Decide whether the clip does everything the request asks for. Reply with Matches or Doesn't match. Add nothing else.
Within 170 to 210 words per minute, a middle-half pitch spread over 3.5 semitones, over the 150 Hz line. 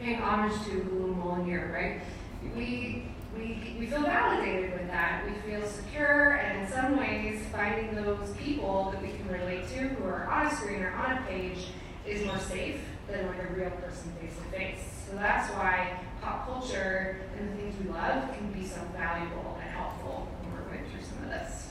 Doesn't match